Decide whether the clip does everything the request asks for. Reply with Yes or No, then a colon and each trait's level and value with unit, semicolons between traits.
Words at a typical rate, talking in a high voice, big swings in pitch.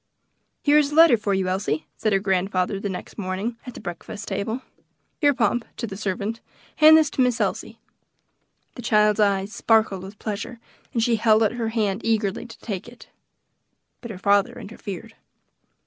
No: average, 180 wpm; high, 215 Hz; average, 3.2 semitones